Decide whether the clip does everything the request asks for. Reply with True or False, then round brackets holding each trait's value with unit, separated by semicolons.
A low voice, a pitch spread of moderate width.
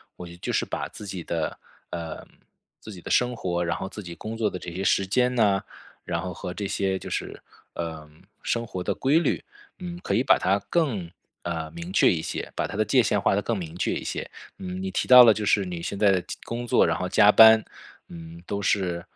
True (95 Hz; 4.2 semitones)